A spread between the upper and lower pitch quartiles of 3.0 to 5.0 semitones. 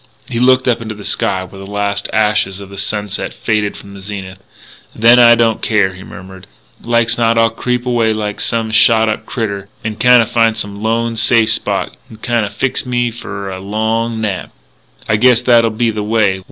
No: narrow, 2.4 semitones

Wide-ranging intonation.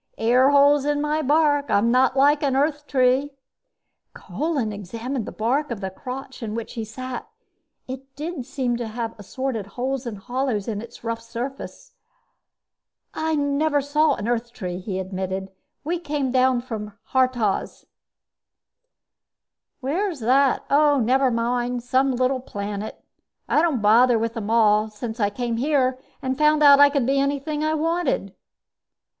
No: average, 3.9 semitones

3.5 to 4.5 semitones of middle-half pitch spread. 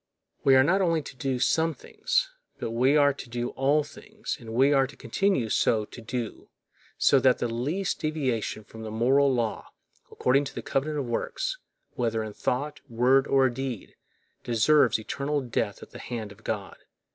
Yes: average, 4.1 semitones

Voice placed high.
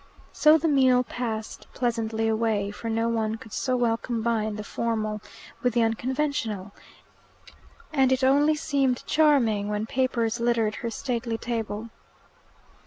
Yes: high, 230 Hz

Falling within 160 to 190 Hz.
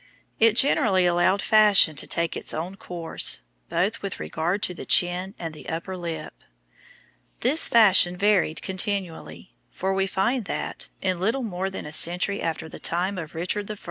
Yes: medium, 185 Hz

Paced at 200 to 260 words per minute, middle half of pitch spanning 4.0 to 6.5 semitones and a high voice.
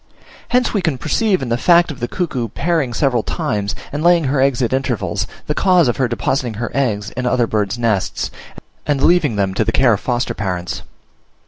No: fast, 205 wpm; average, 5.2 semitones; low, 125 Hz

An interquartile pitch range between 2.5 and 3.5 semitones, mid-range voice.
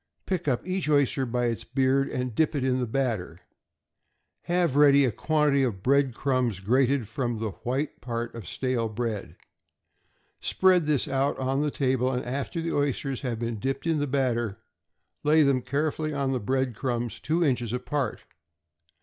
No: average, 3.0 semitones; low, 130 Hz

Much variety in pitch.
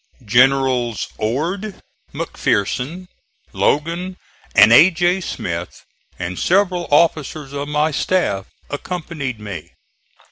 Yes: wide, 6.6 semitones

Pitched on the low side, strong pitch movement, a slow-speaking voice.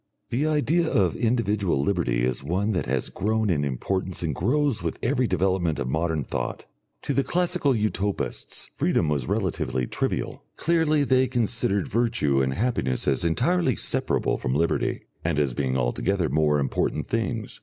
No: very low, 95 Hz; wide, 9.0 semitones; average, 155 wpm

